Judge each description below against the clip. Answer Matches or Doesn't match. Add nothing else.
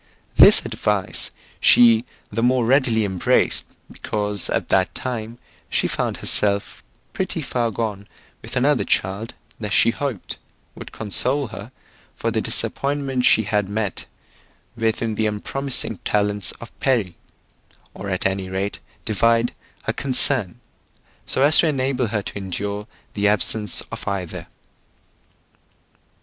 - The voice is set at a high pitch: Doesn't match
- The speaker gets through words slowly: Matches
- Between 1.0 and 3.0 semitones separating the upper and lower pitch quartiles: Doesn't match